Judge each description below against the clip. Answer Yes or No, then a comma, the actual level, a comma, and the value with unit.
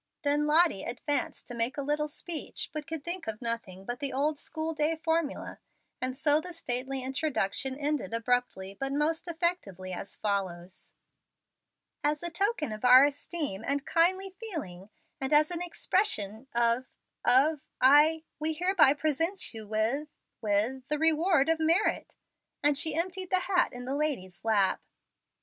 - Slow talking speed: No, average, 155 wpm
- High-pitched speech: Yes, very high, 290 Hz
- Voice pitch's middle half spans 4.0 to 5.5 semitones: Yes, average, 5.2 semitones